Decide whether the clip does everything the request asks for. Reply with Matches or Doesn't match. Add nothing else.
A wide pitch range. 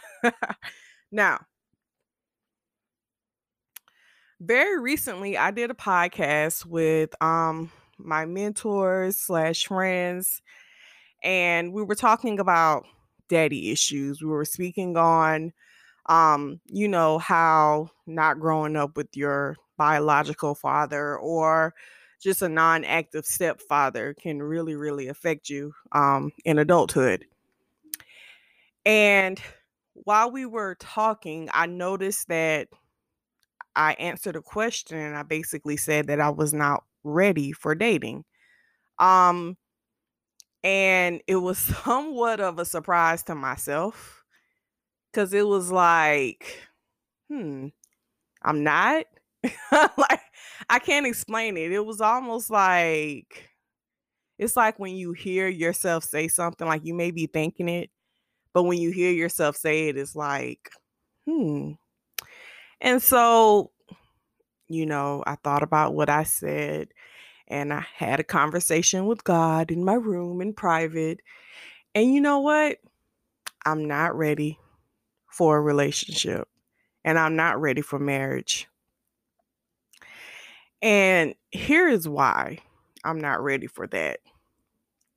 Doesn't match